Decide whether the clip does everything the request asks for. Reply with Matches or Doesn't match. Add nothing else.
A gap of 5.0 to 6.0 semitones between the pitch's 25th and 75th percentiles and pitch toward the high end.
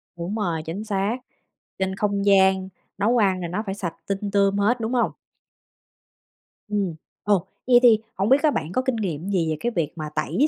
Doesn't match